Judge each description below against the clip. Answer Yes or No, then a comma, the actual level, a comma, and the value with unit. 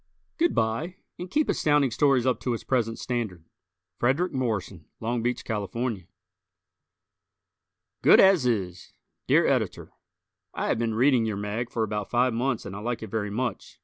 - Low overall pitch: Yes, low, 120 Hz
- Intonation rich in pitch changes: No, average, 3.2 semitones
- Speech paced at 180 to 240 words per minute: No, average, 160 wpm